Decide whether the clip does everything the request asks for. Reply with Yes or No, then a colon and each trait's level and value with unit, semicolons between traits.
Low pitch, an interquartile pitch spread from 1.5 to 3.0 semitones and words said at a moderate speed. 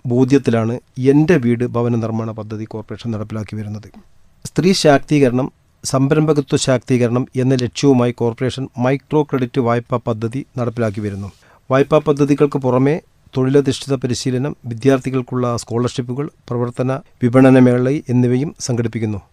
Yes: low, 125 Hz; average, 2.7 semitones; average, 100 wpm